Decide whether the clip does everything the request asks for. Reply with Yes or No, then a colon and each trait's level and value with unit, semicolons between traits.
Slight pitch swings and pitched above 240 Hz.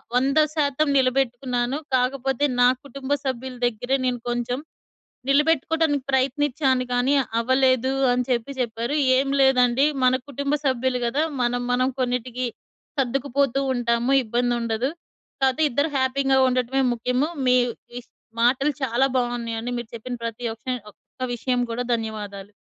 Yes: narrow, 2.0 semitones; very high, 255 Hz